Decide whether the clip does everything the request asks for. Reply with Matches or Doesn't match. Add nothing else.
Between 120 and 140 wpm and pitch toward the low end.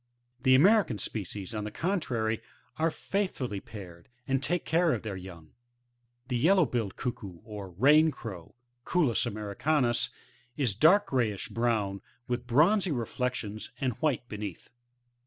Matches